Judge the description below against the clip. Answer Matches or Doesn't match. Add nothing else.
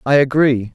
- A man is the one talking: Matches